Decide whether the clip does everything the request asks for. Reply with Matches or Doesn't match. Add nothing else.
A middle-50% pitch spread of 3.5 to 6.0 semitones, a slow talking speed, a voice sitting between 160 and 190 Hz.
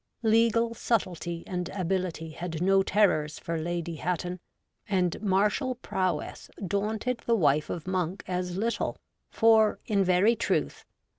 Matches